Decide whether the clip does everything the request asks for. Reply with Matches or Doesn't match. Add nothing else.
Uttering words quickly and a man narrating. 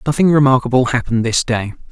Doesn't match